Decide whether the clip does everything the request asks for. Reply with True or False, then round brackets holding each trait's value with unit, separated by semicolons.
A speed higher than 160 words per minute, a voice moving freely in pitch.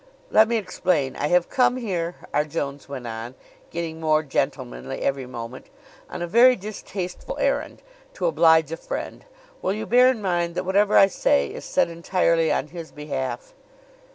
True (170 wpm; 5.7 semitones)